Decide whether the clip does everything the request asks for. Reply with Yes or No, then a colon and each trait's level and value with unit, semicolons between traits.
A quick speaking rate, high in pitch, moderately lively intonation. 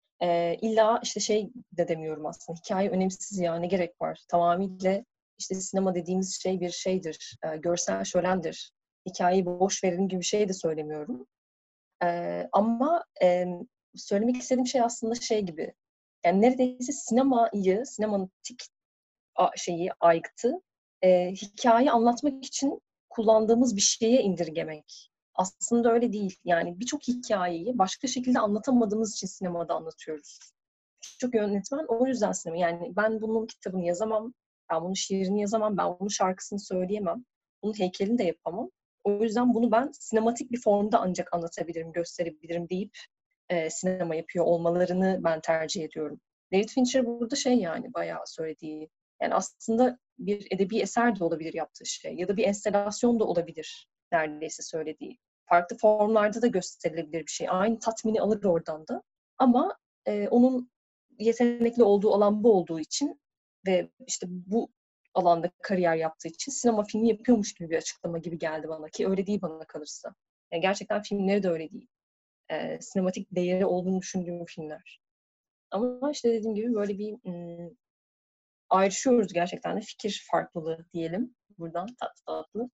Yes: fast, 145 wpm; high, 195 Hz; average, 5.0 semitones